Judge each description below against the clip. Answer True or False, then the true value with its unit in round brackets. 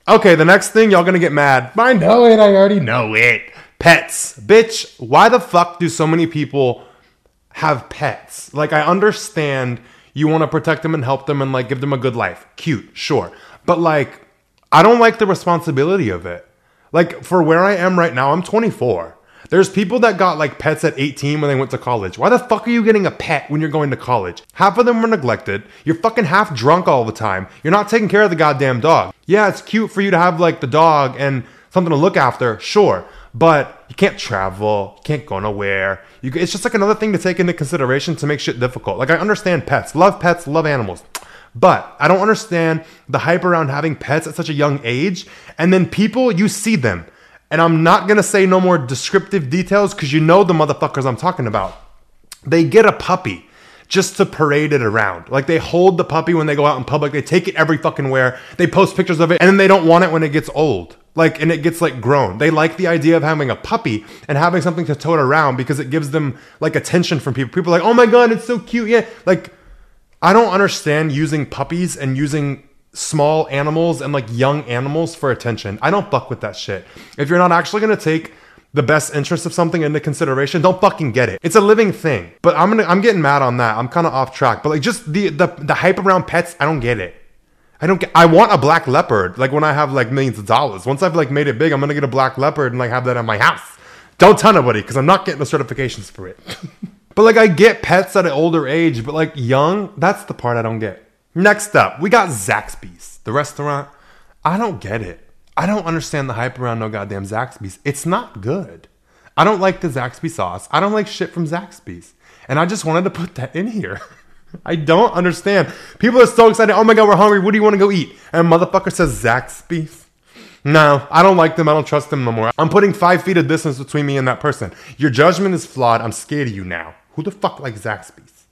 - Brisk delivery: True (240 wpm)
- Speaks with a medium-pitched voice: True (160 Hz)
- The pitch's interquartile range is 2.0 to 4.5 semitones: False (5.3 semitones)